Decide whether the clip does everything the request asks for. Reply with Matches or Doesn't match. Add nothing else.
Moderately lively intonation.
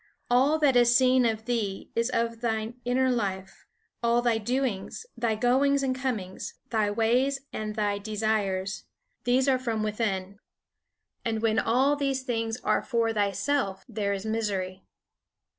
Matches